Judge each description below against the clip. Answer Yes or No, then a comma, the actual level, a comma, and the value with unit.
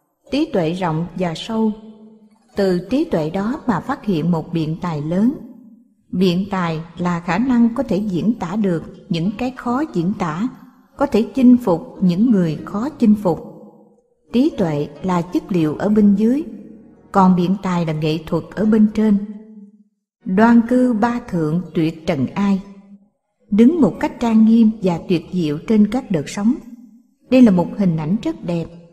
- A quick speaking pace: No, average, 170 wpm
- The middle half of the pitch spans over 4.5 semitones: Yes, average, 5.0 semitones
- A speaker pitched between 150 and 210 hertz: Yes, high, 205 Hz